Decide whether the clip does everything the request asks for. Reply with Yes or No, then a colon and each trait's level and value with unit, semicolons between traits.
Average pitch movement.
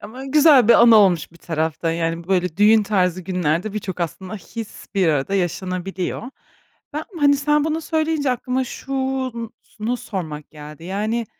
No: wide, 6.6 semitones